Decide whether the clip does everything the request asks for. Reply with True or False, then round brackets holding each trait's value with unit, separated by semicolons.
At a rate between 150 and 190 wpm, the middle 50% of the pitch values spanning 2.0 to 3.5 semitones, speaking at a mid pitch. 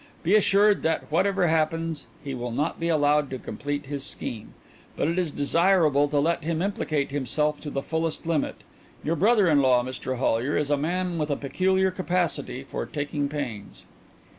True (180 wpm; 3.1 semitones; 150 Hz)